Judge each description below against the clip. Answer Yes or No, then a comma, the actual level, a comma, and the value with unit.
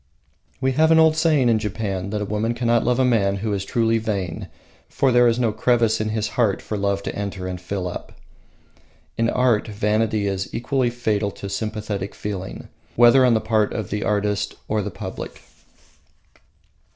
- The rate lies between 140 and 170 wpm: No, average, 185 wpm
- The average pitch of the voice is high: No, low, 110 Hz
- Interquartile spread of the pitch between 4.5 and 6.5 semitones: No, average, 2.9 semitones